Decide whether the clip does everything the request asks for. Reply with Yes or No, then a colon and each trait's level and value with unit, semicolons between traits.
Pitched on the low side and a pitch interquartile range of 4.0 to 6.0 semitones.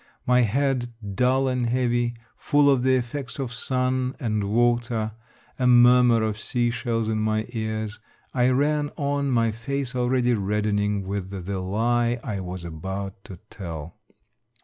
No: low, 120 Hz; average, 3.3 semitones